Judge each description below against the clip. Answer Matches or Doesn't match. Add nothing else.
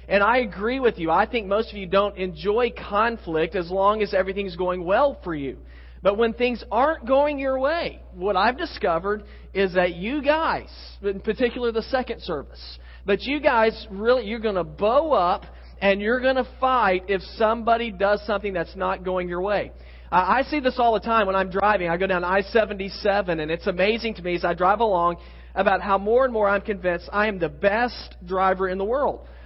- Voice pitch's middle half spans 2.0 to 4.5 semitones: Matches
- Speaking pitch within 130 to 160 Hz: Doesn't match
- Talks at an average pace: Doesn't match